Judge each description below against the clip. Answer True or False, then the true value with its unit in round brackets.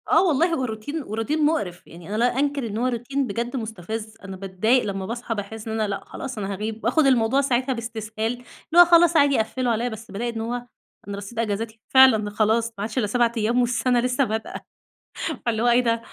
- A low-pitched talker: False (230 Hz)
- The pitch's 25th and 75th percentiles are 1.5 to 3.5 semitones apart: True (2.8 semitones)